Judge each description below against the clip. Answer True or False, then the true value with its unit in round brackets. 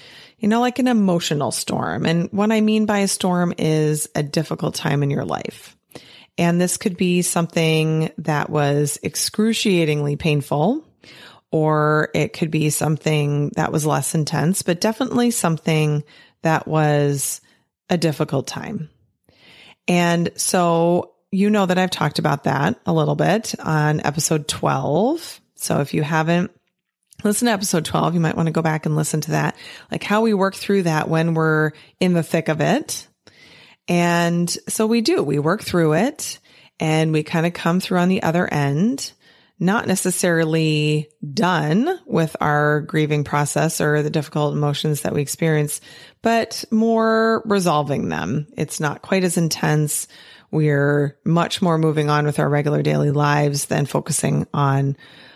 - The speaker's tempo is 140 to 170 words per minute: True (160 wpm)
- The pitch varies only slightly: False (3.7 semitones)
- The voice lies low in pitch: False (160 Hz)